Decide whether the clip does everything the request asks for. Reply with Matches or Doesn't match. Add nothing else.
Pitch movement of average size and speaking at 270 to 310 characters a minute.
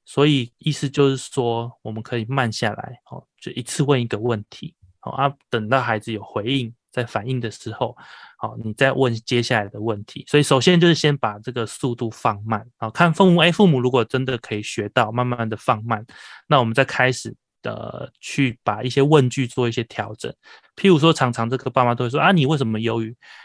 Matches